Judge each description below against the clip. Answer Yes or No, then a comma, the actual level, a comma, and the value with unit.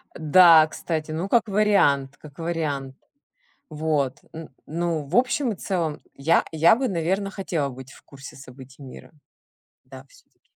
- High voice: No, medium, 160 Hz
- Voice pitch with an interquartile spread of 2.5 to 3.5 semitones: No, average, 4.9 semitones